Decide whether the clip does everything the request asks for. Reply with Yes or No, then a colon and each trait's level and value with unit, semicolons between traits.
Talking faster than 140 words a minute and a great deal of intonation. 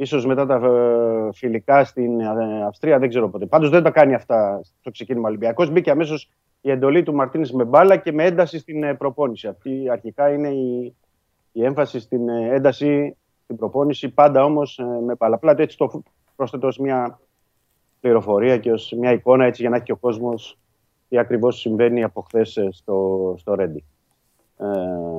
No: average, 165 wpm; average, 3.7 semitones